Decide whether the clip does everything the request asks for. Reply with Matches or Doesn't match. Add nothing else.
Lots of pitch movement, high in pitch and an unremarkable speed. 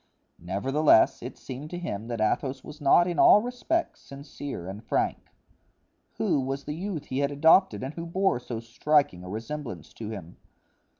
Doesn't match